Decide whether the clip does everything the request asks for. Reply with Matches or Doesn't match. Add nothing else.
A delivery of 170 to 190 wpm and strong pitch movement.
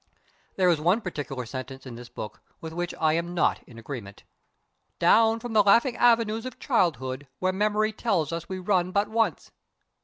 Matches